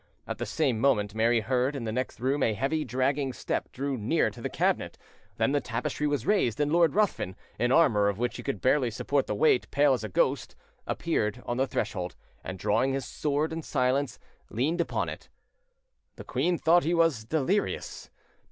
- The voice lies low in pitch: Yes, low, 130 Hz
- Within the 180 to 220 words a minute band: Yes, average, 190 wpm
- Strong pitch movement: No, average, 4.2 semitones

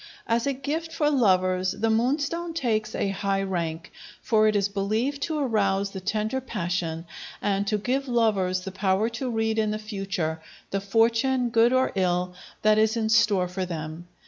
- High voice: Yes, high, 215 Hz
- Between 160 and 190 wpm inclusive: Yes, average, 175 wpm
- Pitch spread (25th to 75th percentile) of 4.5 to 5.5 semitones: No, average, 3.8 semitones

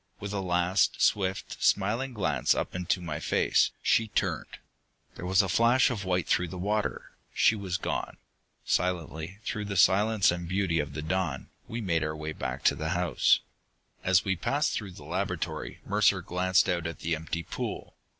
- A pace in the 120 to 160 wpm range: No, average, 180 wpm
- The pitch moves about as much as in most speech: Yes, average, 3.1 semitones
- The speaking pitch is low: Yes, very low, 90 Hz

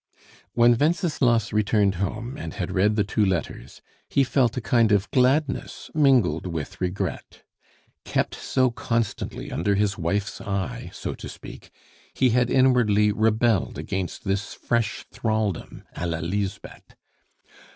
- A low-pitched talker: Yes, low, 105 Hz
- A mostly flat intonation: No, average, 3.7 semitones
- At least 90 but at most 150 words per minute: Yes, slow, 135 wpm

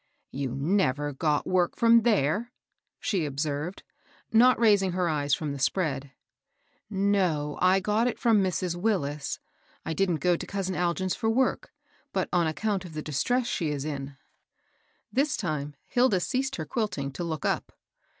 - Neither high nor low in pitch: Yes, medium, 180 Hz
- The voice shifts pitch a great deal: Yes, wide, 6.0 semitones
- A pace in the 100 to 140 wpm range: No, average, 170 wpm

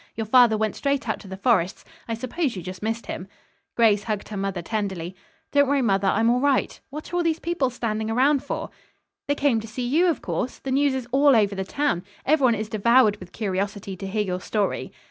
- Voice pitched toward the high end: Yes, high, 225 Hz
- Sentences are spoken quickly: Yes, fast, 220 wpm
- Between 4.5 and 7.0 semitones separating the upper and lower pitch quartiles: Yes, average, 5.1 semitones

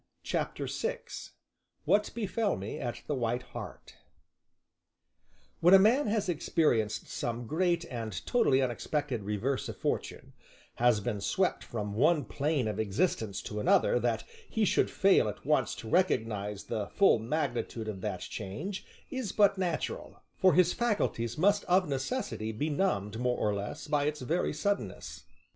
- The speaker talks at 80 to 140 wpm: No, average, 150 wpm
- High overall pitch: No, medium, 145 Hz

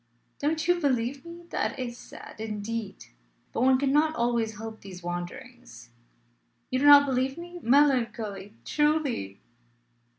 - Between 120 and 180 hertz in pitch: No, very high, 255 Hz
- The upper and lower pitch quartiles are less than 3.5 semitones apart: No, average, 4.7 semitones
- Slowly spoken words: Yes, slow, 130 wpm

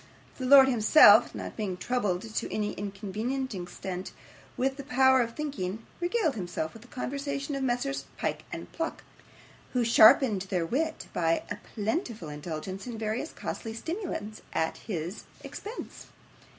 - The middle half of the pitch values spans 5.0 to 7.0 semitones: Yes, wide, 5.6 semitones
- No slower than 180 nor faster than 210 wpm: No, average, 145 wpm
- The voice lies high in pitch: Yes, high, 230 Hz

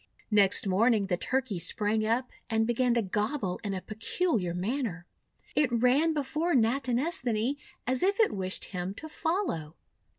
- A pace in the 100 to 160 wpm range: Yes, average, 145 wpm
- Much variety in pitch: Yes, wide, 5.7 semitones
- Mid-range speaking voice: No, high, 230 Hz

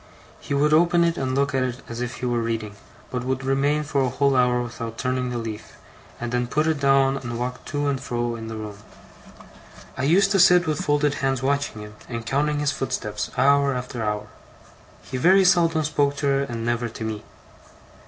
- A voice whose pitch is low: Yes, low, 130 Hz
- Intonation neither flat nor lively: Yes, average, 3.3 semitones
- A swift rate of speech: Yes, fast, 210 wpm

